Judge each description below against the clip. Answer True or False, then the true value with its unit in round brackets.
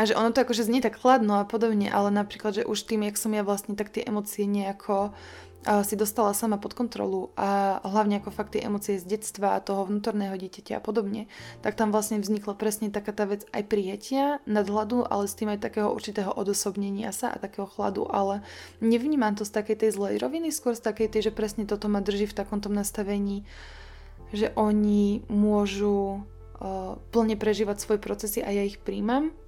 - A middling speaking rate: False (195 wpm)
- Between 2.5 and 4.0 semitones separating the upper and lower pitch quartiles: False (1.3 semitones)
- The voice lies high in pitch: True (210 Hz)